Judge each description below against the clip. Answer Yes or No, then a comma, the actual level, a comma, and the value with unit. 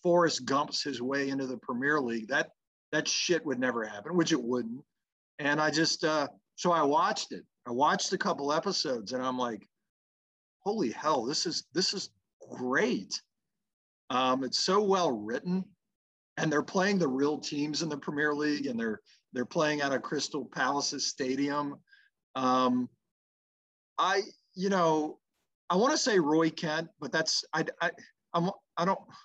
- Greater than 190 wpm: No, average, 165 wpm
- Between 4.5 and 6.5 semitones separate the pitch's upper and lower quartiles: Yes, average, 5.2 semitones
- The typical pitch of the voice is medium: Yes, medium, 150 Hz